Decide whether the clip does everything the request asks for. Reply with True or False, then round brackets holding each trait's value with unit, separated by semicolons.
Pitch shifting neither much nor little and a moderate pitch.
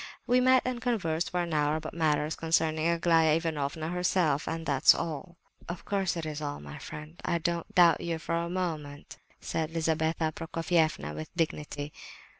False (1.9 semitones; 165 Hz)